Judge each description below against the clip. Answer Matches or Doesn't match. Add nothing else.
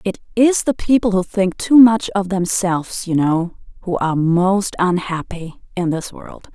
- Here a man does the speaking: Doesn't match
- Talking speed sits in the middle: Matches